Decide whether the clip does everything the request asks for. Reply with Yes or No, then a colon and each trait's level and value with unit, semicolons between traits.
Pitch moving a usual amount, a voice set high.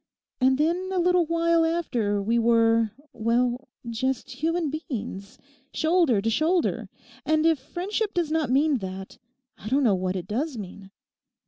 No: wide, 6.4 semitones; very high, 265 Hz